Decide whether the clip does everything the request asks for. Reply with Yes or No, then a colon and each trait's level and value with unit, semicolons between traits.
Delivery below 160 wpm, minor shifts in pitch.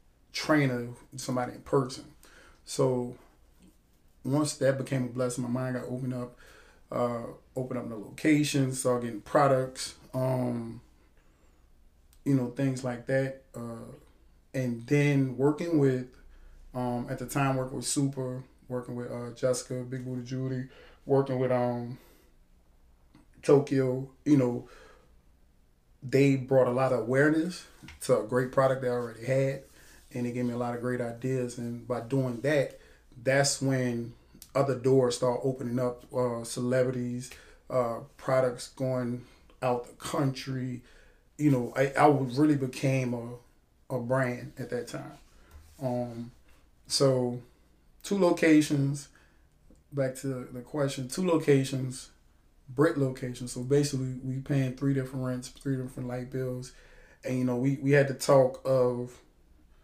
Yes: average, 140 wpm; narrow, 1.8 semitones